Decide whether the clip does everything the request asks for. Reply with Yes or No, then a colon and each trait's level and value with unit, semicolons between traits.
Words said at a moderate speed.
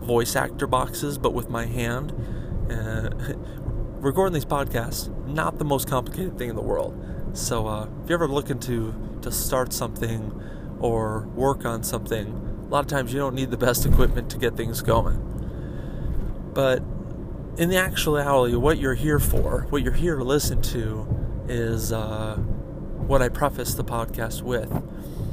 Yes: average, 160 wpm